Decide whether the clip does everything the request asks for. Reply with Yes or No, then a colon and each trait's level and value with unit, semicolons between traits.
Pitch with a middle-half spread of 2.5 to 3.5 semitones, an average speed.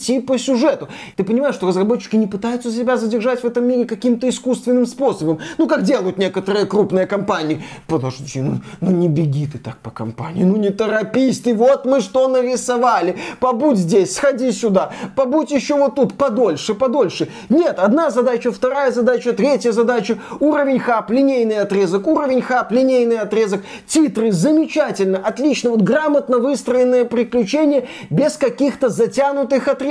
No: average, 4.3 semitones; average, 150 wpm